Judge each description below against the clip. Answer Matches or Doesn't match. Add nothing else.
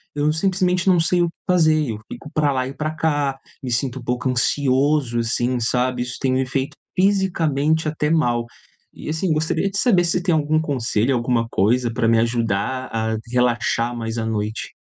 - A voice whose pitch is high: Doesn't match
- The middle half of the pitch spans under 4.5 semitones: Doesn't match